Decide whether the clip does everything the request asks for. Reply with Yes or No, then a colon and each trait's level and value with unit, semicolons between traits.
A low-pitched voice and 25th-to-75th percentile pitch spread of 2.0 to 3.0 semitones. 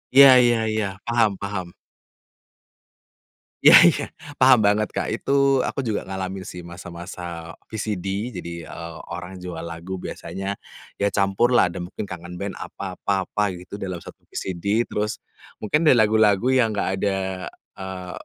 No: very low, 95 Hz; average, 3.4 semitones